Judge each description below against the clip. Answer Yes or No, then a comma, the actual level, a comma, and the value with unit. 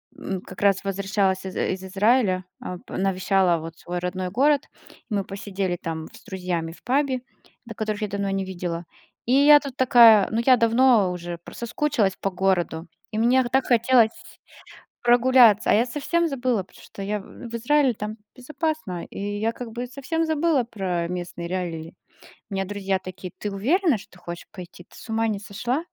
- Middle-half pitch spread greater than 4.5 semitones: Yes, average, 5.0 semitones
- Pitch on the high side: Yes, high, 205 Hz